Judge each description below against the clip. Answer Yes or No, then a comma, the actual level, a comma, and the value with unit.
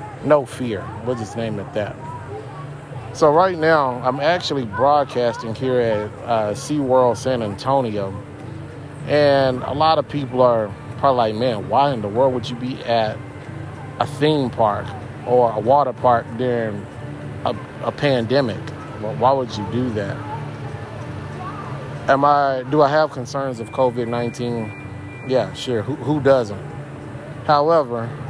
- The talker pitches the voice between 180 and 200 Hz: No, low, 130 Hz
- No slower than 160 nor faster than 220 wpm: No, average, 150 wpm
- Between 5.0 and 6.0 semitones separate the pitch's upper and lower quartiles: No, average, 3.4 semitones